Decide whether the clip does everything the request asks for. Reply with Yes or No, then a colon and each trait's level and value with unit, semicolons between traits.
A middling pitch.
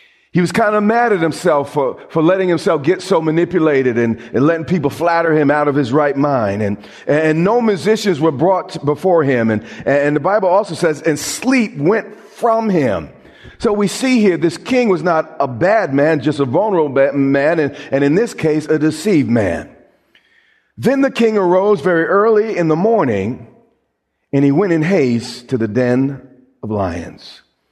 Yes: medium, 160 Hz